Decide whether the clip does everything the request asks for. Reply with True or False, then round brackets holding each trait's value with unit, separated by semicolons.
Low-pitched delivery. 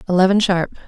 False (190 Hz)